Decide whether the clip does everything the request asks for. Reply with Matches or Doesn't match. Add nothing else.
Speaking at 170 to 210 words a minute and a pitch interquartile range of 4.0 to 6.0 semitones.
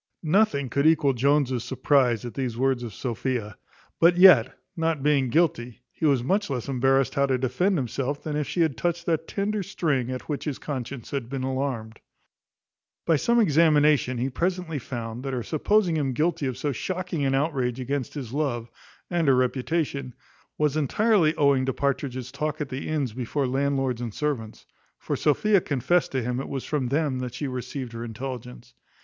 Doesn't match